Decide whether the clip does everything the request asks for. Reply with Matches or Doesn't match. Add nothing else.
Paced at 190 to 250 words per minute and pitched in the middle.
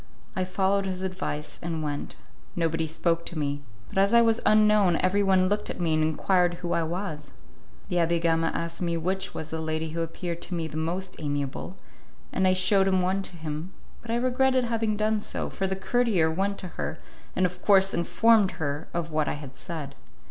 Matches